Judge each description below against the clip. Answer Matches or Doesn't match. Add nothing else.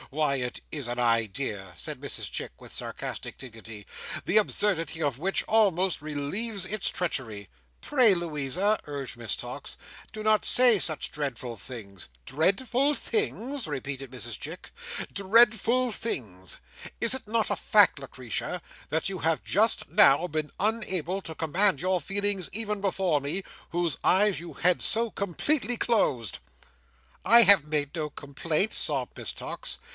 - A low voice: Doesn't match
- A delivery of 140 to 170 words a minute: Matches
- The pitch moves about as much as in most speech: Doesn't match